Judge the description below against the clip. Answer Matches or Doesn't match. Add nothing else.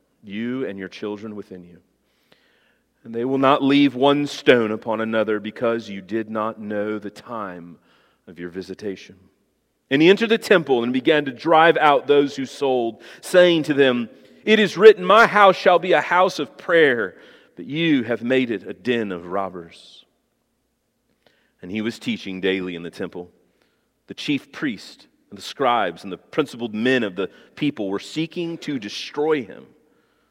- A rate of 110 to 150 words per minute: Doesn't match